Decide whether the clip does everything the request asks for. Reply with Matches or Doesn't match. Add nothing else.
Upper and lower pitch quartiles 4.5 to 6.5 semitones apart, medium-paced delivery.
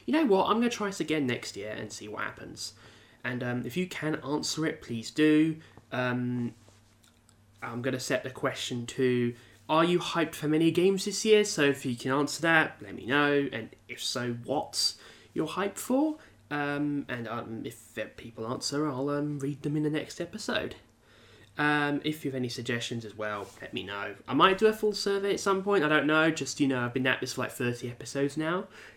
Doesn't match